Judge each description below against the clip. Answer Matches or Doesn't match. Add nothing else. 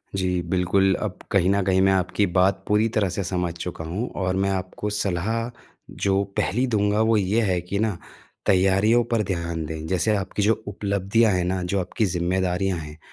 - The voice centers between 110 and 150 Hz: Doesn't match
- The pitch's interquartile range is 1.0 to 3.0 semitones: Matches